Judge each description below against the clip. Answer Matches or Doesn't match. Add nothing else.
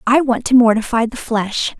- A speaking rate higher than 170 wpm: Matches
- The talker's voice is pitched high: Matches